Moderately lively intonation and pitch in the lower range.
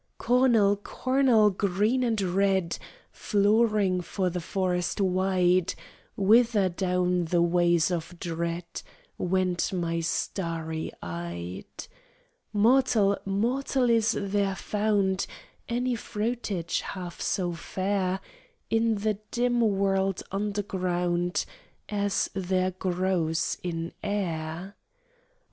No: average, 3.0 semitones; high, 190 Hz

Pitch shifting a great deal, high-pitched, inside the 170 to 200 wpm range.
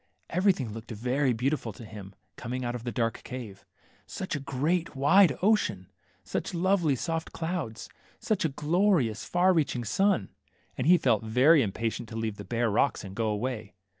No: wide, 6.7 semitones; low, 130 Hz; average, 180 wpm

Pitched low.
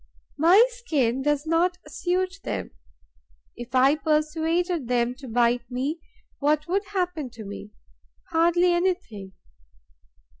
No: very high, 310 Hz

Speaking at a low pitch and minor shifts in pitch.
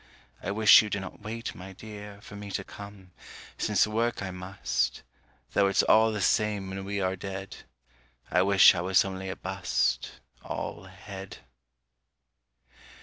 Yes: low, 100 Hz; narrow, 1.5 semitones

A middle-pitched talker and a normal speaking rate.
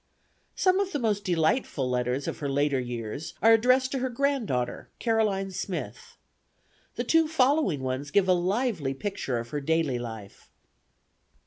Yes: medium, 180 Hz; average, 150 wpm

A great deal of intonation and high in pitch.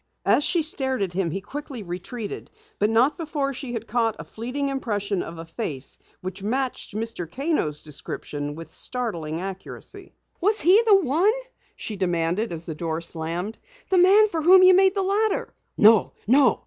Yes: wide, 9.0 semitones; high, 225 Hz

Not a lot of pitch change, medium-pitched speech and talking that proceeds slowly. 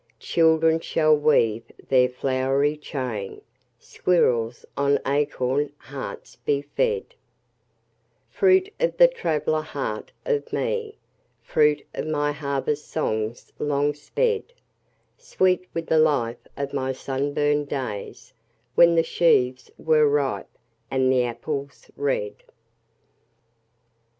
No: average, 3.4 semitones; medium, 145 Hz; slow, 110 wpm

